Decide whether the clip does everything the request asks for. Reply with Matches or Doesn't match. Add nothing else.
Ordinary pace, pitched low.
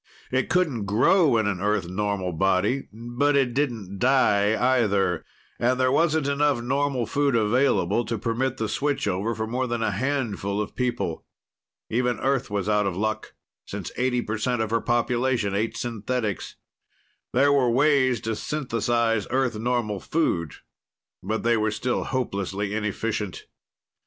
Matches